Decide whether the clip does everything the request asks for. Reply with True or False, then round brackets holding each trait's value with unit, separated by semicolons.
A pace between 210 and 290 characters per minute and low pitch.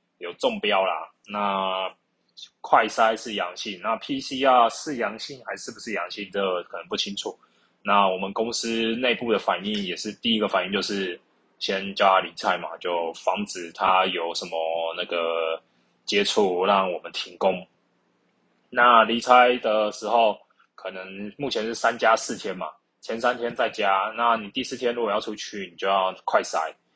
True (240 characters per minute; 100 Hz)